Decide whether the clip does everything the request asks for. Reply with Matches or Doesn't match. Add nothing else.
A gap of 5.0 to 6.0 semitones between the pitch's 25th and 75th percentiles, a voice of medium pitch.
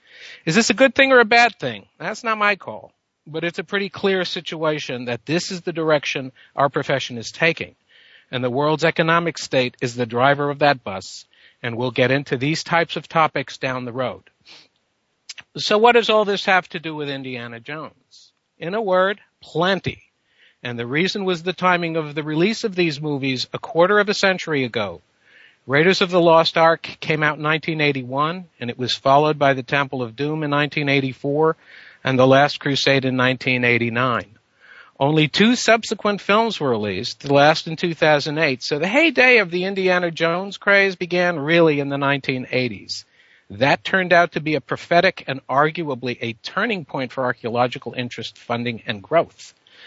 Matches